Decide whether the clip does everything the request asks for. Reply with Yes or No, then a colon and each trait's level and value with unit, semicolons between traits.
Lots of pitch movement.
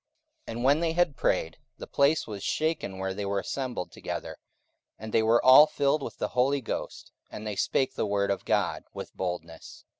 Yes: wide, 5.9 semitones